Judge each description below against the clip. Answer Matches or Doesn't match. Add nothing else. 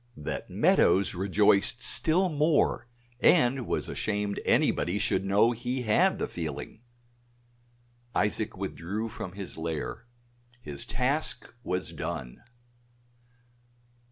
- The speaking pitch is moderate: Doesn't match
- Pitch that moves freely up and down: Doesn't match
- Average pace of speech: Doesn't match